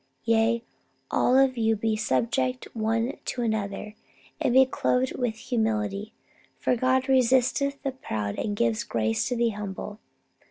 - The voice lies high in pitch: Yes, high, 225 Hz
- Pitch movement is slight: No, average, 3.6 semitones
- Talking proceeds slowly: No, average, 145 wpm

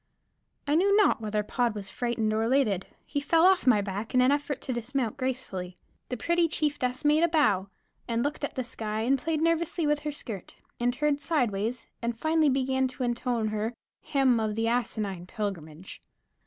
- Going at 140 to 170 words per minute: No, average, 190 wpm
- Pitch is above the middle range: Yes, very high, 250 Hz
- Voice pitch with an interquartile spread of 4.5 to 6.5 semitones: Yes, average, 5.2 semitones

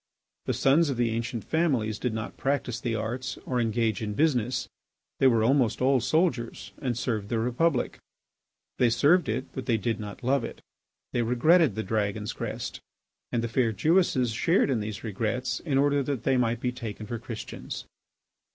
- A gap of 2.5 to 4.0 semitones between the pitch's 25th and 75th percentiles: Yes, average, 3.2 semitones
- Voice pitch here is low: Yes, low, 120 Hz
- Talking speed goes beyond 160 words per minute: Yes, average, 180 wpm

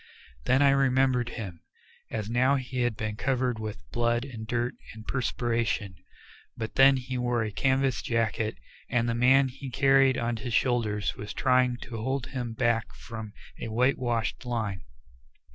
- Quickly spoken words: No, average, 160 wpm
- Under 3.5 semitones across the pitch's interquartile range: Yes, narrow, 2.5 semitones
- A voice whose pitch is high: No, low, 120 Hz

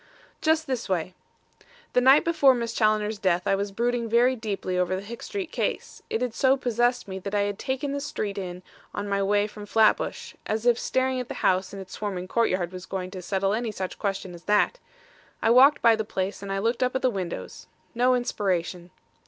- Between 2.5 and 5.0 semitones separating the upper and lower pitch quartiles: Yes, average, 4.2 semitones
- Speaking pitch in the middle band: No, high, 210 Hz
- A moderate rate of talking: No, fast, 215 wpm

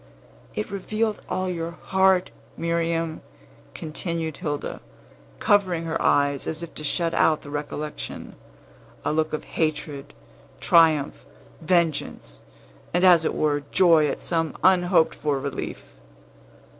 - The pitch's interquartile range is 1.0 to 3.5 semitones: Yes, average, 2.8 semitones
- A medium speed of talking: No, slow, 120 wpm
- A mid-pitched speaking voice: Yes, medium, 165 Hz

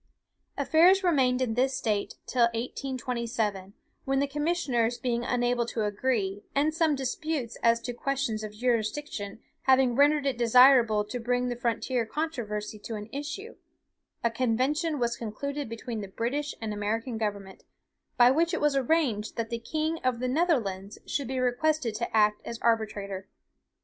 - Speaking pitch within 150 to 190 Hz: No, high, 245 Hz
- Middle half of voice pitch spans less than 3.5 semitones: No, average, 3.9 semitones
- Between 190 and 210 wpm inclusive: No, average, 155 wpm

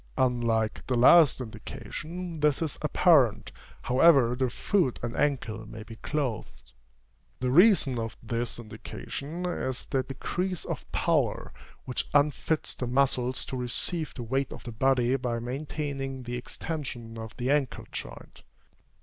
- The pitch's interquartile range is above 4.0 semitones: No, average, 3.7 semitones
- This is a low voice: Yes, low, 130 Hz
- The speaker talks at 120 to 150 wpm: Yes, average, 140 wpm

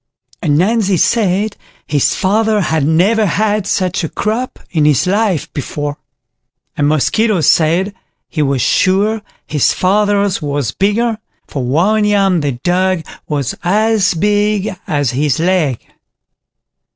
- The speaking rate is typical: No, slow, 125 wpm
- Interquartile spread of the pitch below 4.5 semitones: No, wide, 5.5 semitones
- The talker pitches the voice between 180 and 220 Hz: Yes, medium, 185 Hz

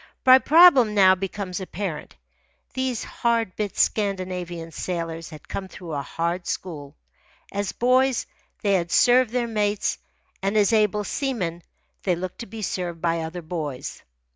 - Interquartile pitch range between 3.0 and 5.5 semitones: Yes, average, 4.5 semitones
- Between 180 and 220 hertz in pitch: Yes, high, 190 Hz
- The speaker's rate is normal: Yes, average, 145 wpm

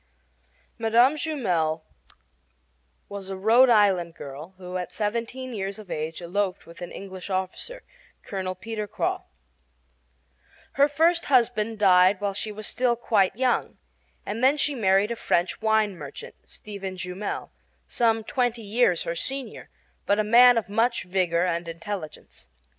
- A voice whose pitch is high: Yes, high, 205 Hz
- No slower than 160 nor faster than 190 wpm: No, average, 140 wpm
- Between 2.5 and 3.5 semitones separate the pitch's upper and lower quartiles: No, average, 4.2 semitones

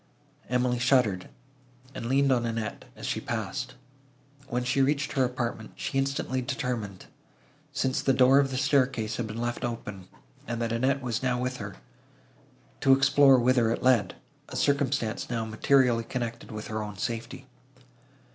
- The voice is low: Yes, low, 125 Hz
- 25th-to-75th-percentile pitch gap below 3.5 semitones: Yes, average, 2.7 semitones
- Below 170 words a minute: Yes, average, 155 wpm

